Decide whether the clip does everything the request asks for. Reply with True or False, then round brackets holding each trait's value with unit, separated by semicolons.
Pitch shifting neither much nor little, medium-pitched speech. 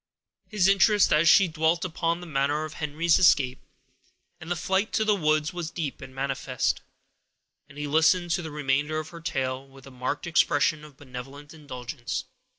True (3.6 semitones; 155 Hz)